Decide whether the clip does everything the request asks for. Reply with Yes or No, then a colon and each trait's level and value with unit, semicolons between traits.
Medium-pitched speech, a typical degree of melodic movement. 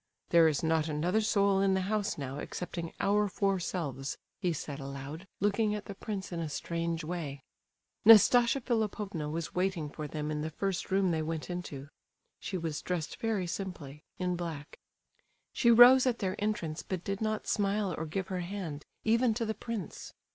Yes: medium, 180 Hz; average, 4.6 semitones